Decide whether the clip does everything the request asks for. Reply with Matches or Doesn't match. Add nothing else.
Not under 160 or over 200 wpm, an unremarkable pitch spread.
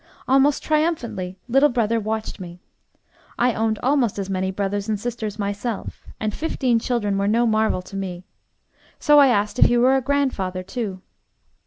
Matches